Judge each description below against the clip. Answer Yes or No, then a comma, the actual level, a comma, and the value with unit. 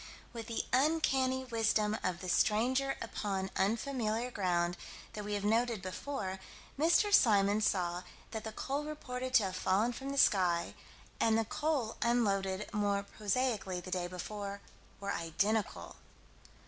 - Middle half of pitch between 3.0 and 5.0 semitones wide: Yes, average, 4.6 semitones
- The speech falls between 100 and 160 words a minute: Yes, average, 140 wpm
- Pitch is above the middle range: Yes, high, 215 Hz